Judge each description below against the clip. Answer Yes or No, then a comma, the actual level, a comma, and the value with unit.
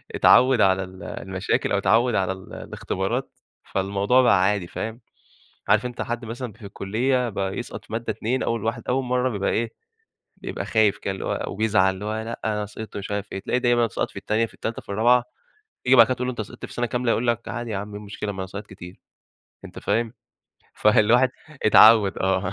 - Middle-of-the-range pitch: No, low, 110 Hz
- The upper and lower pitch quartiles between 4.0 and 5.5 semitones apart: No, average, 3.3 semitones